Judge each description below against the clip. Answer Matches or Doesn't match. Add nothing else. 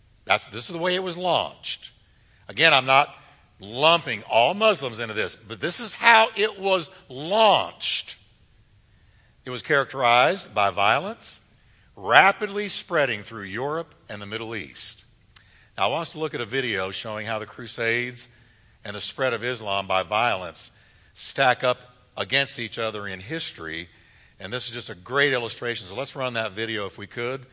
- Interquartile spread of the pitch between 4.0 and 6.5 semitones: Matches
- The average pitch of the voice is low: Matches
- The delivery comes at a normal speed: Matches